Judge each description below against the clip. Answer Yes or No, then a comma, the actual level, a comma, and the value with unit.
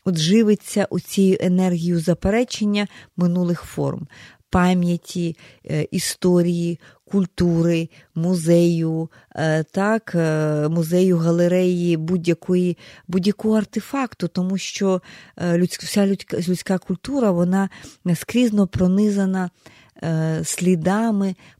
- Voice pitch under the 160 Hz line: No, medium, 180 Hz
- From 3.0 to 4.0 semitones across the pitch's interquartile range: No, narrow, 2.5 semitones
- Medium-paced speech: No, slow, 70 wpm